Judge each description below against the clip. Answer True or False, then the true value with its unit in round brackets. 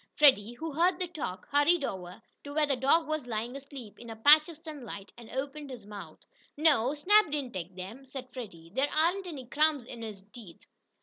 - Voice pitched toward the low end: False (270 Hz)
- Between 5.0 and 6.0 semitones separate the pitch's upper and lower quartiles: True (5.3 semitones)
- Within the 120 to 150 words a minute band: False (200 wpm)